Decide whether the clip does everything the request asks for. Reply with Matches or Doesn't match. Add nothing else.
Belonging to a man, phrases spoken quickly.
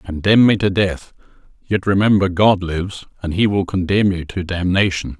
Doesn't match